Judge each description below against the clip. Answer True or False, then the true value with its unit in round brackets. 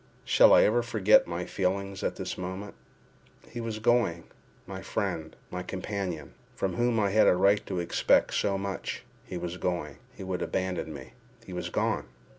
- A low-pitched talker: True (95 Hz)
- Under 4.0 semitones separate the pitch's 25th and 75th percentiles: True (2.6 semitones)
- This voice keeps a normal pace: True (155 wpm)